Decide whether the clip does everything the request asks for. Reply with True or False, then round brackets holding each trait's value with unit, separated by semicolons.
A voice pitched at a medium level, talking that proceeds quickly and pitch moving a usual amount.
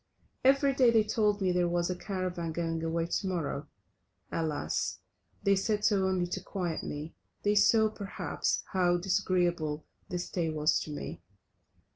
False (180 Hz; 155 wpm; 3.5 semitones)